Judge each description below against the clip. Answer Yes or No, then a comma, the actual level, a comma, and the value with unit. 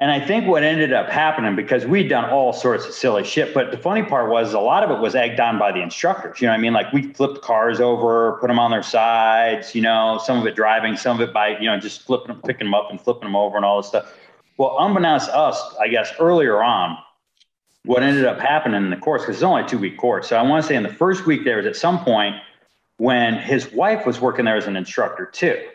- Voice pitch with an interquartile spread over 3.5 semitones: Yes, average, 3.9 semitones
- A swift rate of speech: Yes, fast, 275 wpm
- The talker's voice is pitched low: Yes, low, 120 Hz